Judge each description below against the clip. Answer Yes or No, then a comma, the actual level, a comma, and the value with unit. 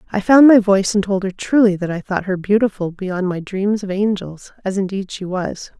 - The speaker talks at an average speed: No, fast, 215 wpm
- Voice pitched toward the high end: Yes, high, 195 Hz